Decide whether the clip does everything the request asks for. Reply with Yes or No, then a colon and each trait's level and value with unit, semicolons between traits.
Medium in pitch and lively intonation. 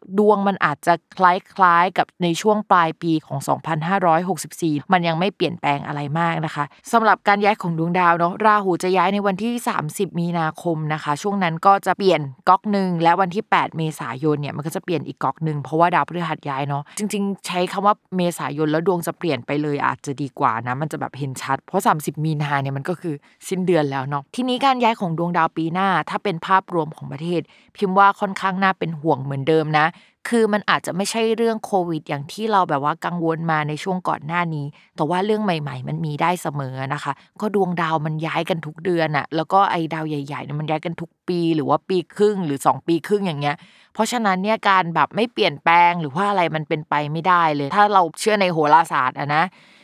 No: medium, 170 Hz; average, 4.0 semitones